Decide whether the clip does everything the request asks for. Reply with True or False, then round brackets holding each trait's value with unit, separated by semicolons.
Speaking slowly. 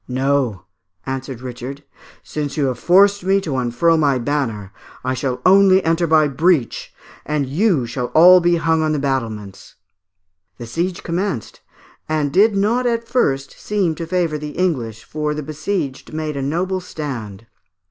False (160 wpm)